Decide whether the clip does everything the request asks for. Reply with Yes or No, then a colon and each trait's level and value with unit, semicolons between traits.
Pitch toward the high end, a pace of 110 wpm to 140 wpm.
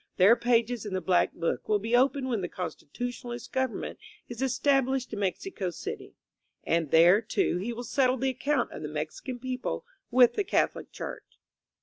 No: high, 240 Hz; average, 175 wpm